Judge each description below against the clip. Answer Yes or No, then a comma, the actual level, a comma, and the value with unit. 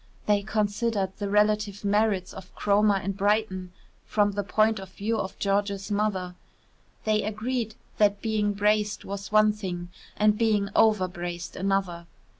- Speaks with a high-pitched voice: Yes, high, 205 Hz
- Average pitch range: No, narrow, 1.6 semitones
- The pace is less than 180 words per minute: Yes, average, 140 wpm